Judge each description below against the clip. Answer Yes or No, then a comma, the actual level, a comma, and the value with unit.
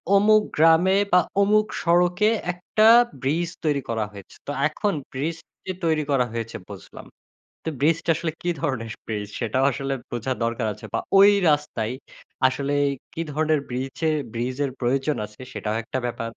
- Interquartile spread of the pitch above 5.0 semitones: Yes, wide, 5.6 semitones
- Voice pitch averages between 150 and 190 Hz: No, medium, 140 Hz